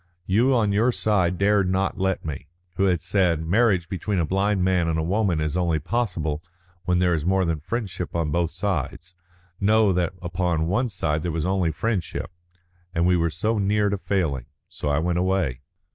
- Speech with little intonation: No, average, 3.2 semitones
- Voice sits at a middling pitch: No, very low, 90 Hz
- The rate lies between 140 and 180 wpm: No, average, 190 wpm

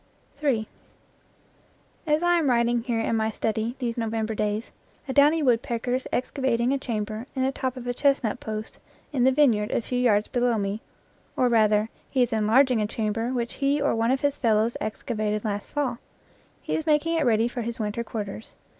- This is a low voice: No, high, 235 Hz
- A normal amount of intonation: Yes, average, 3.2 semitones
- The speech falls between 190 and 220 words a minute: Yes, average, 195 wpm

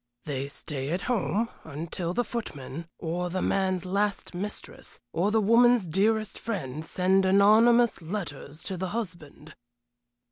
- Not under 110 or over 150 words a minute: Yes, slow, 135 wpm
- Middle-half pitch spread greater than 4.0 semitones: Yes, average, 4.8 semitones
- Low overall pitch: No, medium, 185 Hz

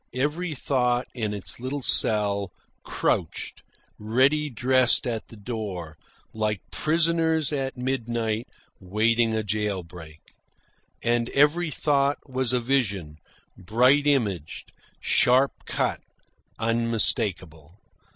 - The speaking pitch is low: Yes, low, 120 Hz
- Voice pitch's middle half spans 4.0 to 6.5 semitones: Yes, average, 4.4 semitones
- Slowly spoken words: Yes, slow, 100 wpm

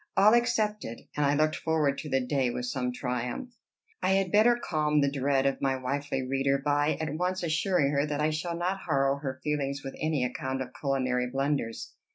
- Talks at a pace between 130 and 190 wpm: No, average, 200 wpm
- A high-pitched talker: No, medium, 145 Hz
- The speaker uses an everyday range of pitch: Yes, average, 3.0 semitones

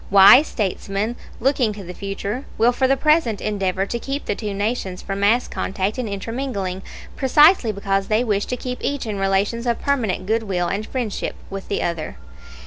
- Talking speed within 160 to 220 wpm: Yes, average, 185 wpm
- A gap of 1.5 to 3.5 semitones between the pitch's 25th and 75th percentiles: No, average, 4.0 semitones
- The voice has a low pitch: No, high, 210 Hz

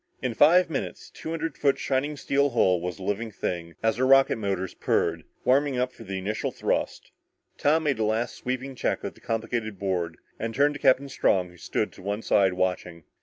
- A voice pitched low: Yes, low, 115 Hz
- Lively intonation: Yes, wide, 6.2 semitones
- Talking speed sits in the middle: No, fast, 210 wpm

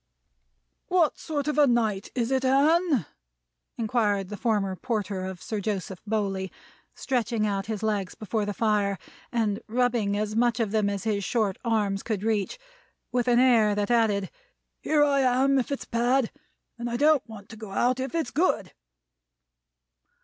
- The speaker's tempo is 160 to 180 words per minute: Yes, average, 165 wpm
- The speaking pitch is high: Yes, high, 225 Hz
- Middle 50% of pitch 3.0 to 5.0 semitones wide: Yes, average, 3.7 semitones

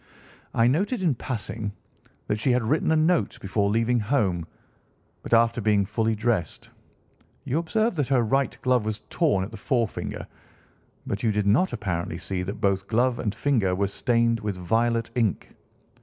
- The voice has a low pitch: Yes, low, 115 Hz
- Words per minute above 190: No, average, 170 wpm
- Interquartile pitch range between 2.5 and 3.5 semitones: No, average, 3.9 semitones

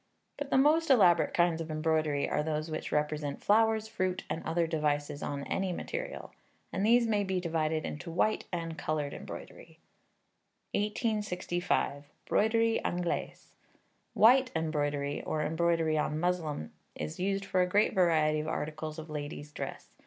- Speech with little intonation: No, average, 4.3 semitones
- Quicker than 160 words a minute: No, average, 145 wpm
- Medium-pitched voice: Yes, medium, 165 Hz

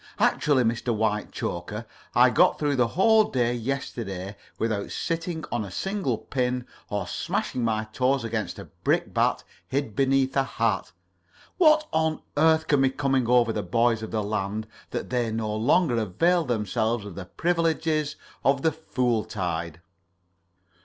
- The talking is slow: No, average, 150 wpm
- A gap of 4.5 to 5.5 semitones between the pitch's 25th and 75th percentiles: Yes, average, 5.2 semitones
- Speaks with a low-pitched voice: Yes, low, 120 Hz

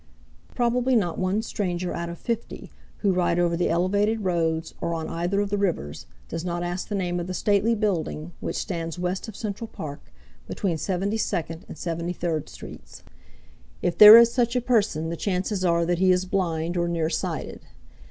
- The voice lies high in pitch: No, medium, 180 Hz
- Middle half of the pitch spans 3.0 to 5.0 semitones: Yes, average, 3.3 semitones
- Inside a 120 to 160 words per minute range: No, average, 185 wpm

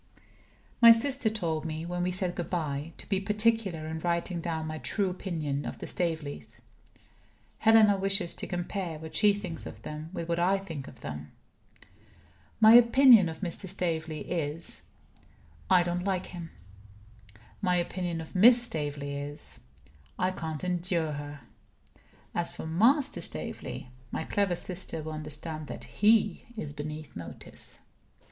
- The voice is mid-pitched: Yes, medium, 170 Hz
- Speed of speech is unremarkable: Yes, average, 150 wpm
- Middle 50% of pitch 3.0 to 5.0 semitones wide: Yes, average, 3.8 semitones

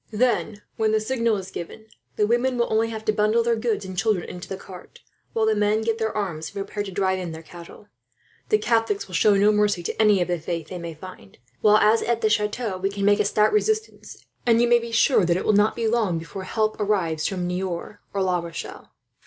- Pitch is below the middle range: No, high, 210 Hz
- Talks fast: Yes, fast, 240 wpm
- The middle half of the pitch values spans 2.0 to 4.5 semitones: Yes, average, 3.1 semitones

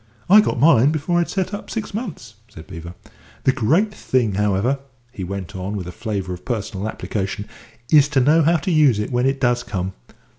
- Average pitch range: No, wide, 7.7 semitones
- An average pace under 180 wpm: No, average, 200 wpm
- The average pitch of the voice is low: Yes, low, 120 Hz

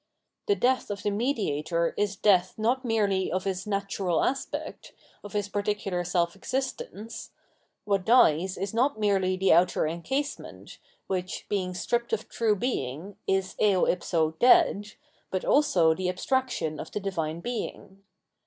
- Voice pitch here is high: Yes, high, 195 Hz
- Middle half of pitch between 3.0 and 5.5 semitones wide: Yes, average, 3.6 semitones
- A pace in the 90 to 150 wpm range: Yes, average, 145 wpm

